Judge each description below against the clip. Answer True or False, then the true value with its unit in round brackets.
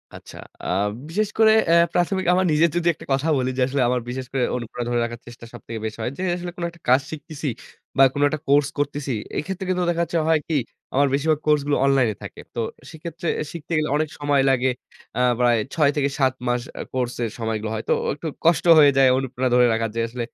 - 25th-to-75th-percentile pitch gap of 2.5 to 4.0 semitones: False (4.5 semitones)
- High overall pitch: False (140 Hz)